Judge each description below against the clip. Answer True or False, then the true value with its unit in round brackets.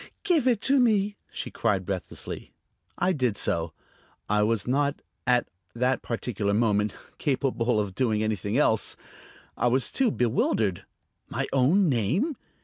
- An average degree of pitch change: False (6.1 semitones)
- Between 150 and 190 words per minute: False (140 wpm)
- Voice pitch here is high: False (120 Hz)